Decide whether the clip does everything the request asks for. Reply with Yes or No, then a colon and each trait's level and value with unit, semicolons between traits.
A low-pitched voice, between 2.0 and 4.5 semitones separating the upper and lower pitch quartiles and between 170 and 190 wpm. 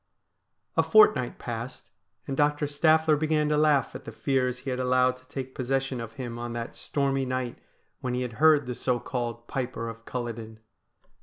Yes: low, 130 Hz; average, 3.1 semitones; average, 180 wpm